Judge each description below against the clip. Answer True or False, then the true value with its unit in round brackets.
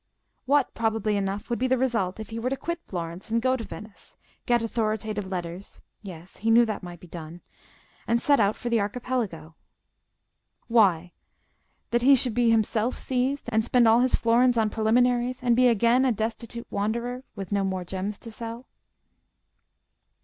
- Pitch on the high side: True (225 Hz)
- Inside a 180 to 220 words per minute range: False (165 wpm)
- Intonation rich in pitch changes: False (3.4 semitones)